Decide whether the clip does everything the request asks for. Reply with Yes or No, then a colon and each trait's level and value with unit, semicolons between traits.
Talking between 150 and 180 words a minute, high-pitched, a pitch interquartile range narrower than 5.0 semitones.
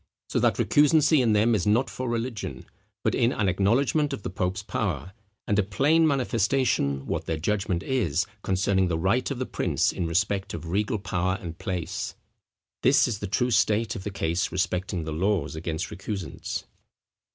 No: average, 175 wpm; low, 100 Hz; average, 4.5 semitones